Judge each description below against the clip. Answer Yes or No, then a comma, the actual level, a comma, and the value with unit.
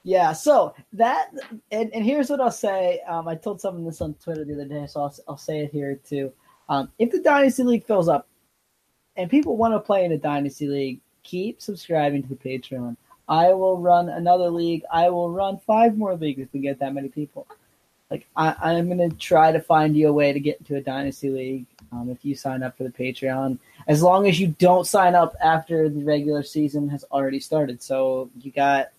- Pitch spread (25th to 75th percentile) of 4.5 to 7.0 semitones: Yes, average, 5.1 semitones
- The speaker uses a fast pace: Yes, fast, 220 wpm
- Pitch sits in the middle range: Yes, medium, 155 Hz